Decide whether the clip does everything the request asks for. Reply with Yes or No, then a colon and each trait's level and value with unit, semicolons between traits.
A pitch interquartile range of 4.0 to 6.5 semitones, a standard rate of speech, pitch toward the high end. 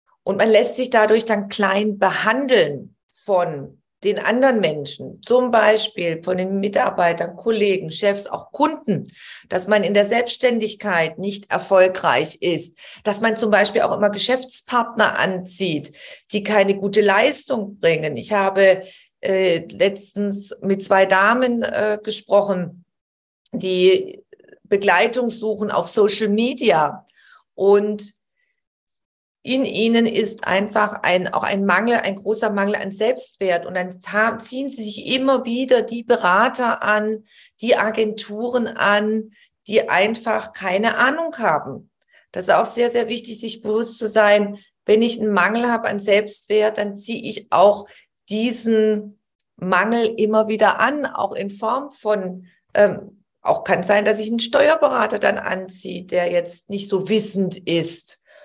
No: average, 2.9 semitones; average, 140 wpm; high, 210 Hz